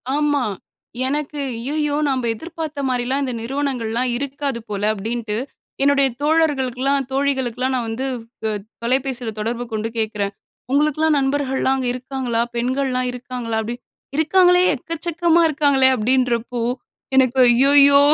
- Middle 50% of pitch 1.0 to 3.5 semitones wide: Yes, average, 3.0 semitones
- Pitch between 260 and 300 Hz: Yes, very high, 265 Hz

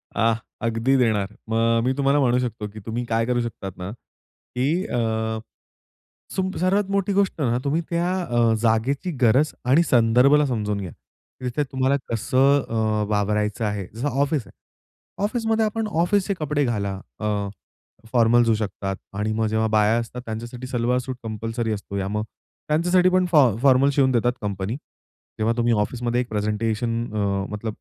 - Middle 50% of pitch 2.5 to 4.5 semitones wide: Yes, average, 4.2 semitones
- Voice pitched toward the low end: Yes, low, 120 Hz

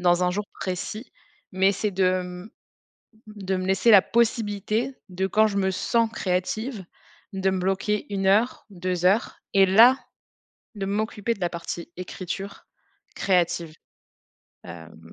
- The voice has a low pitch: No, high, 195 Hz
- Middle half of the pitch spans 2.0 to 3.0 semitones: Yes, narrow, 2.5 semitones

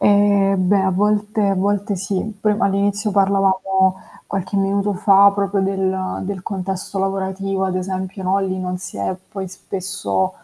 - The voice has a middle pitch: No, high, 195 Hz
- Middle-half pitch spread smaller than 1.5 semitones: Yes, narrow, 1.1 semitones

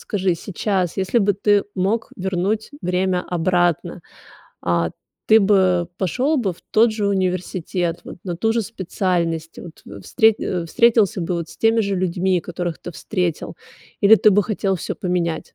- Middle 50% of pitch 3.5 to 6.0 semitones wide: No, average, 2.8 semitones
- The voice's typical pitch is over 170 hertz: Yes, medium, 185 Hz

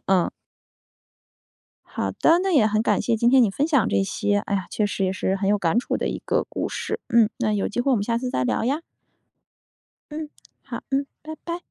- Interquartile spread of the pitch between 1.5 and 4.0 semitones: No, wide, 5.5 semitones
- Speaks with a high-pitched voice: Yes, high, 225 Hz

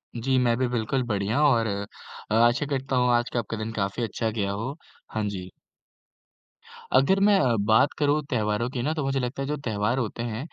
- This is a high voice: No, low, 120 Hz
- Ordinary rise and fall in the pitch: Yes, average, 3.7 semitones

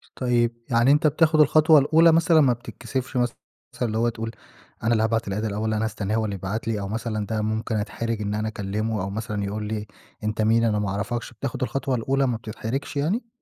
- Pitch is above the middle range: No, low, 115 Hz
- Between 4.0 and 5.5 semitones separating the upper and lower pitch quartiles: No, average, 3.1 semitones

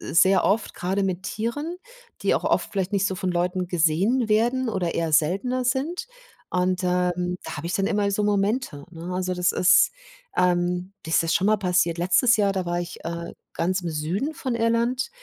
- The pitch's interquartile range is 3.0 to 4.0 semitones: Yes, average, 3.5 semitones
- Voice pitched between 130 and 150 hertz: No, medium, 185 Hz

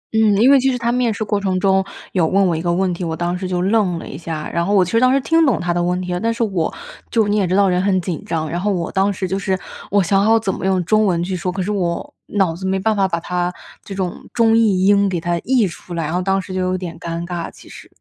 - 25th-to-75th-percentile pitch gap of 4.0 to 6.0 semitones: No, average, 2.7 semitones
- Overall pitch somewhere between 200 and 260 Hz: No, high, 190 Hz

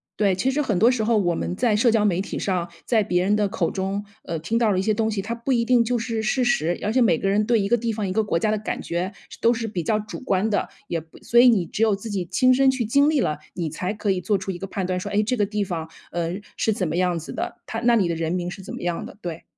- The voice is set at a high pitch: Yes, high, 205 Hz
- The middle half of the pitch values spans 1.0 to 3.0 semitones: No, average, 4.0 semitones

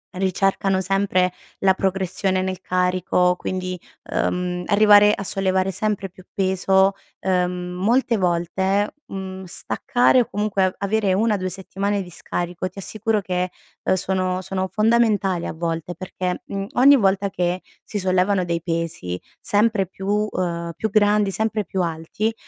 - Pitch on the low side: No, high, 190 Hz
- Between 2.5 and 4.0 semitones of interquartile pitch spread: No, narrow, 1.9 semitones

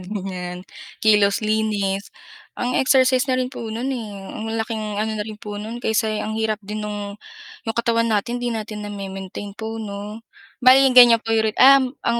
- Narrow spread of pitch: Yes, narrow, 2.2 semitones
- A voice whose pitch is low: No, high, 220 Hz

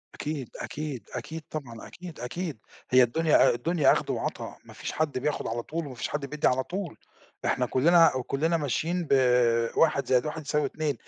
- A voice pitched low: No, medium, 150 Hz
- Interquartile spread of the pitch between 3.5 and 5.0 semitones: Yes, average, 4.1 semitones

